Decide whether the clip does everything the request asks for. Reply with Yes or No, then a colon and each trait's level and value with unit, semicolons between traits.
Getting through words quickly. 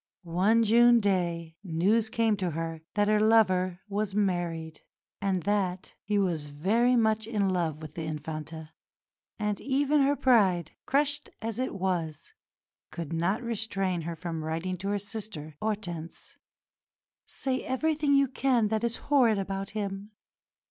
No: average, 145 wpm